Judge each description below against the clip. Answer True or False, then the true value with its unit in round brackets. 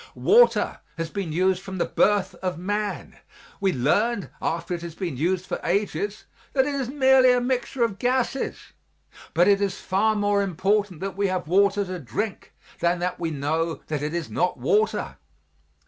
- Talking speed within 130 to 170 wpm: False (180 wpm)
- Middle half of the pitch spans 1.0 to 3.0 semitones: False (3.6 semitones)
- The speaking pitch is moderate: False (195 Hz)